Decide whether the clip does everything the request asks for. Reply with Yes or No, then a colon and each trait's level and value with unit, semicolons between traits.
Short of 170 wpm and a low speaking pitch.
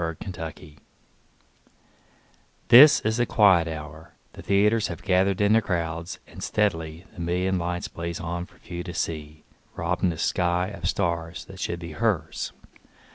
Yes: average, 160 wpm; very low, 85 Hz